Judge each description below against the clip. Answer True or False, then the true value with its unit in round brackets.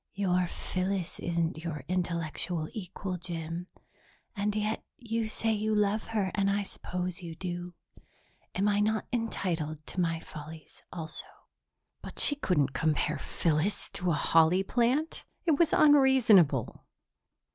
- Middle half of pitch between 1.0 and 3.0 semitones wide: False (4.4 semitones)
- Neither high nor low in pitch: True (180 Hz)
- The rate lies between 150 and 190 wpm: False (135 wpm)